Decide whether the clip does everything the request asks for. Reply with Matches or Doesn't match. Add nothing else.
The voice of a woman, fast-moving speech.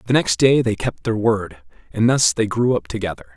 Doesn't match